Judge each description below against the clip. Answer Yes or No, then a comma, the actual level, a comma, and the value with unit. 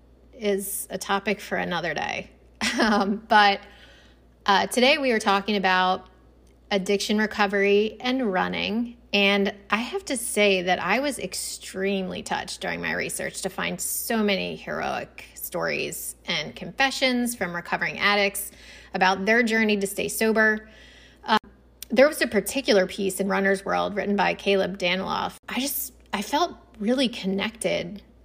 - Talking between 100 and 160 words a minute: Yes, average, 140 wpm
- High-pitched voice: Yes, high, 205 Hz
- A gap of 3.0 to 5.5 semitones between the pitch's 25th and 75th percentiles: No, narrow, 2.4 semitones